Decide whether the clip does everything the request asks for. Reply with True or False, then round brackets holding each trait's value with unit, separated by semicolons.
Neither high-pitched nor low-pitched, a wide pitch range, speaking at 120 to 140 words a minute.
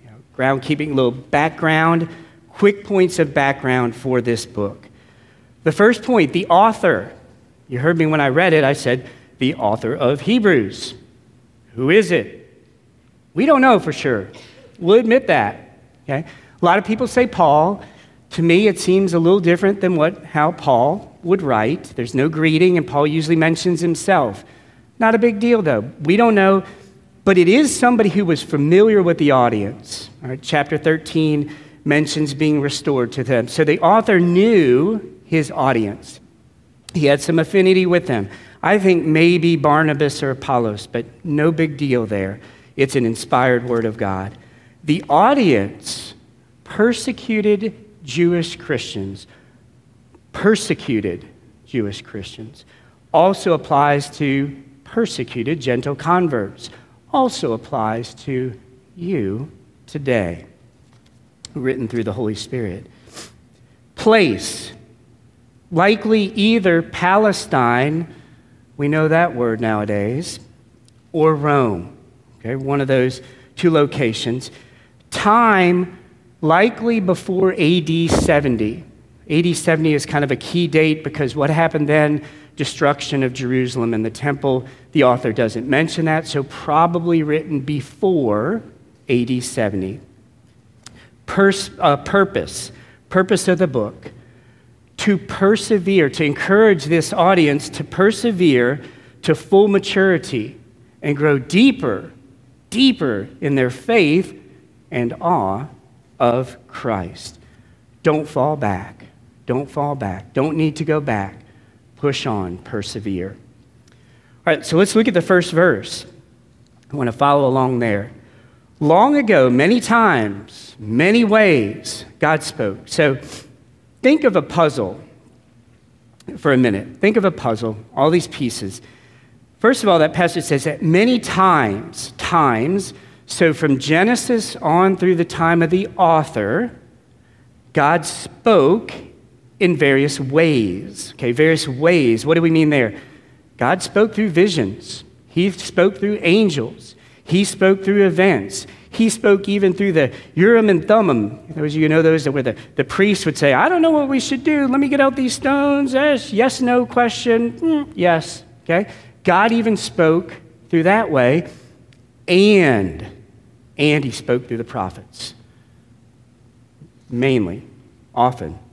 True (150 Hz; 6.8 semitones; 135 wpm)